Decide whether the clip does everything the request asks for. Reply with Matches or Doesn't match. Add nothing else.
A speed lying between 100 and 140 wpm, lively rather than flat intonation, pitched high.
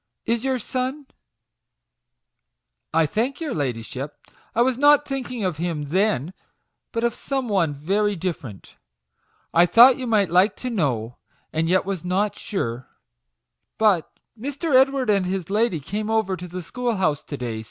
Doesn't match